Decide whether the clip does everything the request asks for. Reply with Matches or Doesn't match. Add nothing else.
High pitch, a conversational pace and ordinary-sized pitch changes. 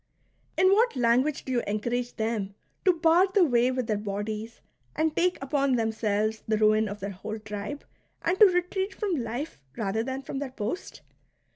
Doesn't match